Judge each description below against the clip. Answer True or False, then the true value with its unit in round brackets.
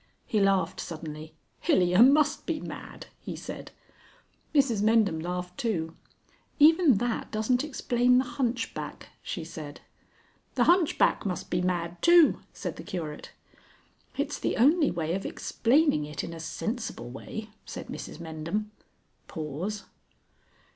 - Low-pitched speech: False (205 Hz)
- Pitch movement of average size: False (7.0 semitones)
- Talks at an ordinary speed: False (130 wpm)